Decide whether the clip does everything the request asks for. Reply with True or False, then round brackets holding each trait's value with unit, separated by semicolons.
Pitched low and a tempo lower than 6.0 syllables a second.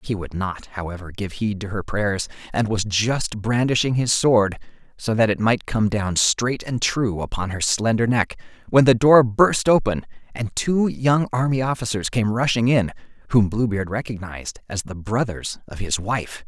True (110 Hz; 4.6 syllables/s)